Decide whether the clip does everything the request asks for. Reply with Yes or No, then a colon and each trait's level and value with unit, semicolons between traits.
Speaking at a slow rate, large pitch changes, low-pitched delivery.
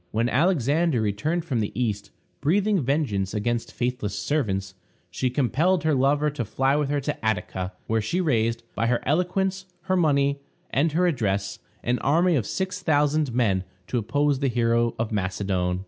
No: average, 165 wpm; wide, 5.8 semitones; low, 130 Hz